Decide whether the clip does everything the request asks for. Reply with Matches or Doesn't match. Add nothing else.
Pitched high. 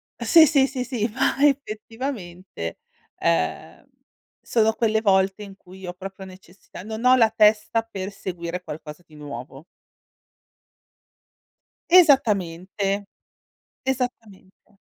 Matches